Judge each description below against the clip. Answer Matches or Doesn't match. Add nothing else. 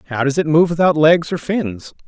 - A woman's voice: Doesn't match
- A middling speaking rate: Doesn't match